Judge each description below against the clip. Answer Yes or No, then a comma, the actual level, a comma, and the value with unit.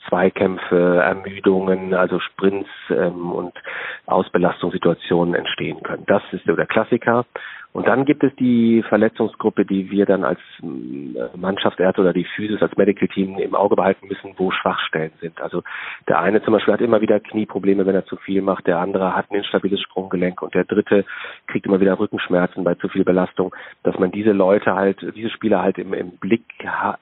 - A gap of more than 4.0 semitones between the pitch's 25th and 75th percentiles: No, narrow, 2.6 semitones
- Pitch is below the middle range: Yes, very low, 95 Hz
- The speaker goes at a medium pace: Yes, average, 180 wpm